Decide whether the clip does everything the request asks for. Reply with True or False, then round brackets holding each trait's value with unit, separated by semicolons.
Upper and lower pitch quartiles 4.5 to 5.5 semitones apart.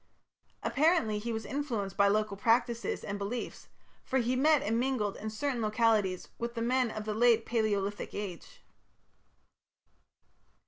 False (3.0 semitones)